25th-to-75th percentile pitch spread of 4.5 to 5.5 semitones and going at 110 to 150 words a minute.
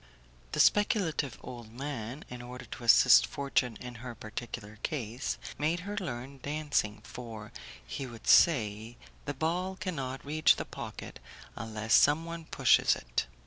Yes: average, 5.2 semitones; average, 140 wpm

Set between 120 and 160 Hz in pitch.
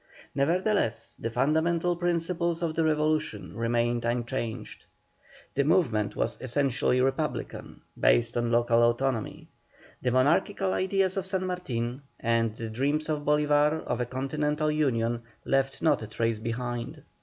Yes: low, 135 Hz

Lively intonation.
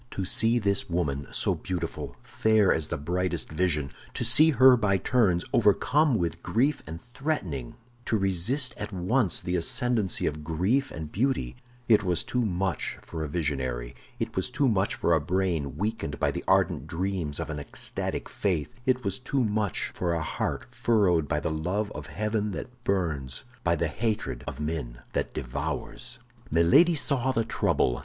Yes: wide, 6.4 semitones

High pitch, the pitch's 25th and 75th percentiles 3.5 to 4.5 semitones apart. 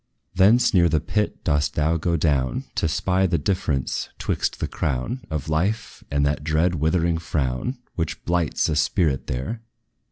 No: very low, 80 Hz; average, 3.8 semitones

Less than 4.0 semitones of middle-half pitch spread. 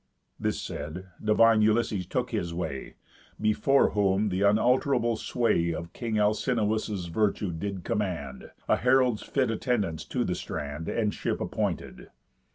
No: average, 4.5 semitones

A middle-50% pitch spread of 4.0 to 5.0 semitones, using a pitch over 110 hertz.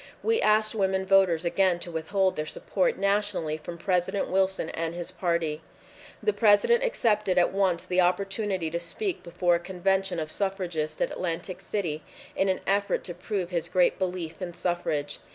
No: narrow, 2.6 semitones; medium, 185 Hz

